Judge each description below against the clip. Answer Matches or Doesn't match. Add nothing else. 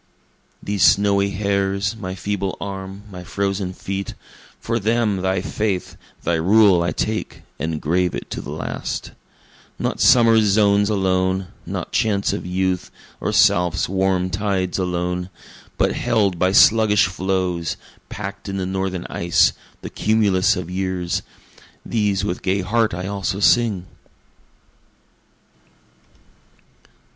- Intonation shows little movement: Matches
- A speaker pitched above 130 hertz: Doesn't match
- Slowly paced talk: Matches